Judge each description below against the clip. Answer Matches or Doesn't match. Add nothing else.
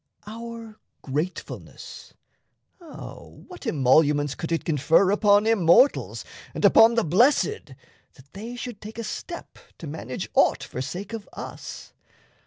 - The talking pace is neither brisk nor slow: Doesn't match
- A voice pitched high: Matches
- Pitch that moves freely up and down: Matches